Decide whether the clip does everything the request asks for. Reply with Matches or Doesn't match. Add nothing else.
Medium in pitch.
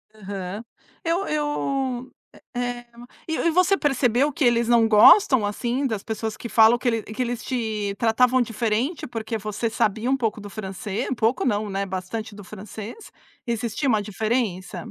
Doesn't match